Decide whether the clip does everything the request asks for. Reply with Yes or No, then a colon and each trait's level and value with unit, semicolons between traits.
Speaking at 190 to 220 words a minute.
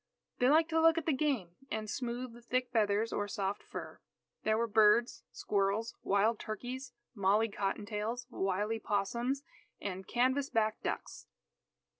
No: average, 150 wpm